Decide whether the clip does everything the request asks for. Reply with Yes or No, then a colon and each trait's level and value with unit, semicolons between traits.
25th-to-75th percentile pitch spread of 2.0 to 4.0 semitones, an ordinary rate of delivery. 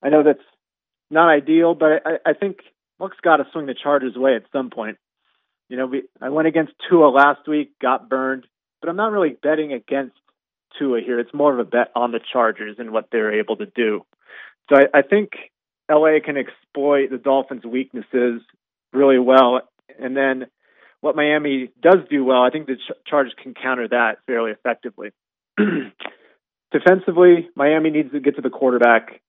Yes: average, 3.5 semitones; average, 185 wpm